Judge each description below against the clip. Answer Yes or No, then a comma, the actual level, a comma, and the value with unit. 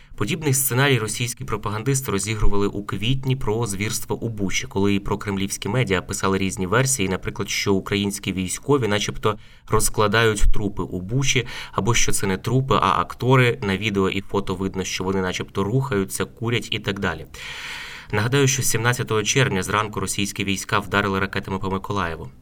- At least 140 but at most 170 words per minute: Yes, fast, 155 wpm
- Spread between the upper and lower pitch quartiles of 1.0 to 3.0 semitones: No, average, 3.5 semitones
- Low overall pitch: Yes, low, 105 Hz